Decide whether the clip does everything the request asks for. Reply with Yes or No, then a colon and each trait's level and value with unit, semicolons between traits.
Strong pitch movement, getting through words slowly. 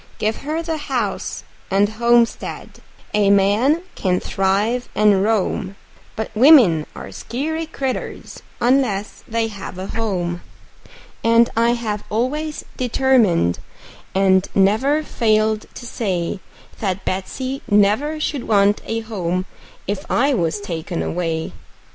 No: average, 4.4 semitones; slow, 120 wpm